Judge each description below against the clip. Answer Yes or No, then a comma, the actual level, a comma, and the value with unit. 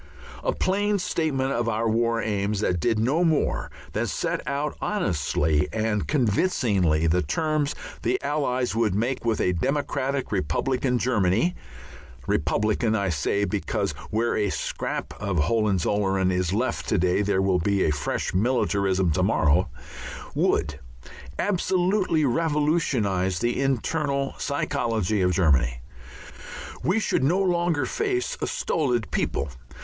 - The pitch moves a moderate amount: No, wide, 7.2 semitones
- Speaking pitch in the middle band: No, low, 115 Hz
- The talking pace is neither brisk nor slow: No, slow, 130 wpm